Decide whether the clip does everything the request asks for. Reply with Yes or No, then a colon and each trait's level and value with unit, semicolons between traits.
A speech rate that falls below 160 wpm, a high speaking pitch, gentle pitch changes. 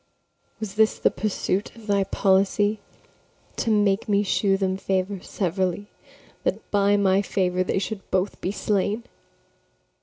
Yes: average, 140 wpm; high, 200 Hz; narrow, 1.5 semitones